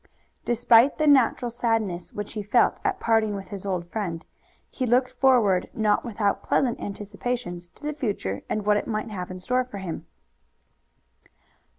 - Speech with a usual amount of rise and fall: Yes, average, 3.7 semitones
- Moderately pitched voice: No, high, 215 Hz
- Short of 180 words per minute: Yes, average, 165 wpm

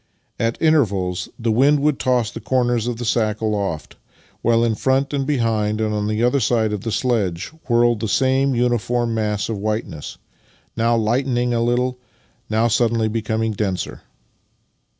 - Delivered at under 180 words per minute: Yes, average, 160 wpm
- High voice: No, low, 115 Hz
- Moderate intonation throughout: No, narrow, 2.3 semitones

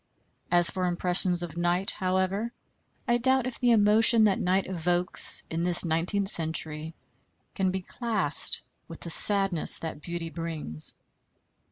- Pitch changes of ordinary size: Yes, average, 3.3 semitones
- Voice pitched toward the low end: No, medium, 180 Hz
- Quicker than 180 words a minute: No, average, 140 wpm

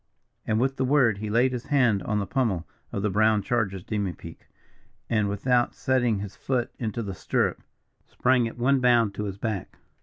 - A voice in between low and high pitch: No, low, 110 Hz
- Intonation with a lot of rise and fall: No, average, 3.4 semitones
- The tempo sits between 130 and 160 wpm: No, average, 185 wpm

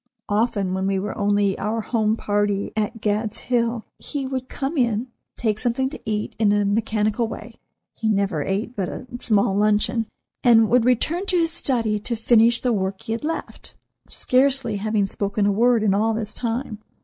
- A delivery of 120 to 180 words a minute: Yes, average, 175 wpm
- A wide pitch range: No, average, 2.8 semitones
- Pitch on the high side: Yes, high, 220 Hz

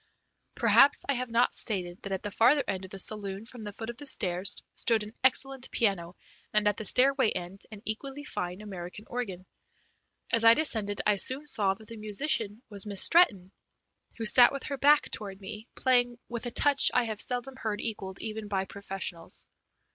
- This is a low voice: No, high, 215 Hz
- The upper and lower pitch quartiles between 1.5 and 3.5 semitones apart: No, average, 4.0 semitones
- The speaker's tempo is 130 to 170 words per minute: No, average, 195 wpm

